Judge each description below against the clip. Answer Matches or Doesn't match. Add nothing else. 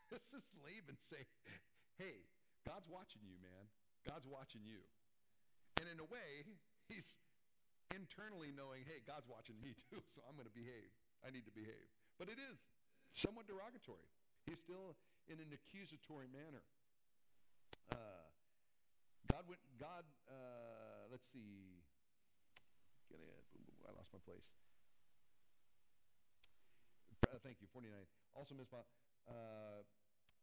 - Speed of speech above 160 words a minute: Doesn't match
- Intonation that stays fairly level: Doesn't match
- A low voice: Matches